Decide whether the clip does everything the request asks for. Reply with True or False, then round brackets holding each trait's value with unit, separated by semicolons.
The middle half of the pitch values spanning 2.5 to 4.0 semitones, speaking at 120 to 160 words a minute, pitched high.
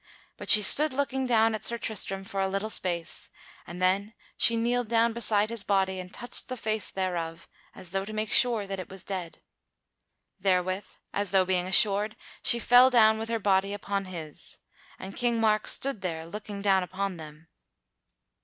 False (3.2 semitones; 180 wpm; 200 Hz)